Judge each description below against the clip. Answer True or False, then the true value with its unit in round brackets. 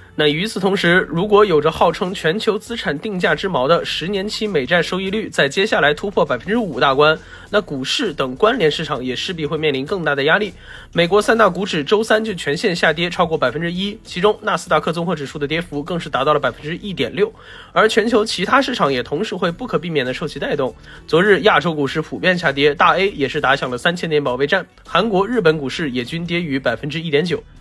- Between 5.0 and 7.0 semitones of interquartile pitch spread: True (5.5 semitones)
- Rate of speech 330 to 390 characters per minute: True (350 characters per minute)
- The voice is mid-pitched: True (170 Hz)